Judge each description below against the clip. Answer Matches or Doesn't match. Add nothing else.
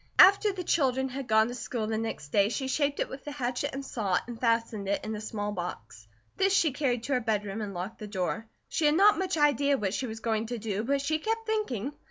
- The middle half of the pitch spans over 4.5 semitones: Matches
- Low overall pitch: Doesn't match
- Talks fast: Matches